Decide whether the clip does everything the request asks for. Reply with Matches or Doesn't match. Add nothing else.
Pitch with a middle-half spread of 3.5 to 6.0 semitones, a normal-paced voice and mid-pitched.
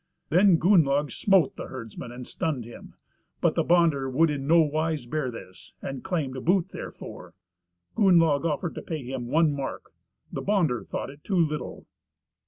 Matches